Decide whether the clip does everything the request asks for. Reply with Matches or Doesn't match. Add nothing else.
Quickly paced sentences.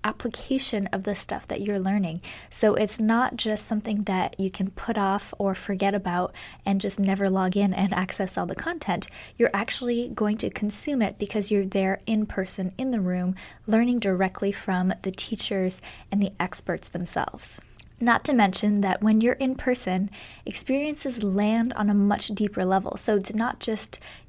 Doesn't match